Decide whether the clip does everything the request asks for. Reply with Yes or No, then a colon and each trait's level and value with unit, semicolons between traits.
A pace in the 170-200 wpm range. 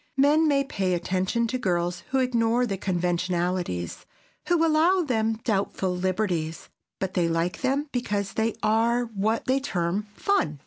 No: average, 145 wpm